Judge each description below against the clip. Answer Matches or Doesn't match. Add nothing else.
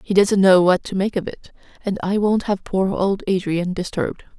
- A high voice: Matches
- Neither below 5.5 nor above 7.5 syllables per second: Doesn't match